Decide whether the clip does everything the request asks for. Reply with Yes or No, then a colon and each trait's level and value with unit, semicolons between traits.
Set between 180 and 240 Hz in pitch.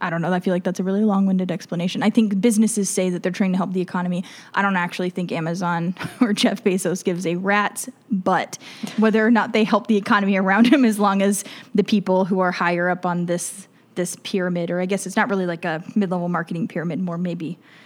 Yes: high, 190 Hz